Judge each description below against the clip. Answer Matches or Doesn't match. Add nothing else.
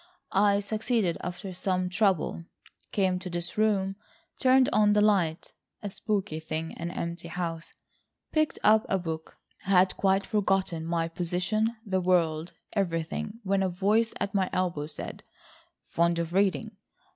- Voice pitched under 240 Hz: Matches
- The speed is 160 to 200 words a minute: Doesn't match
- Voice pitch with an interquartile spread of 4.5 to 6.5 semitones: Doesn't match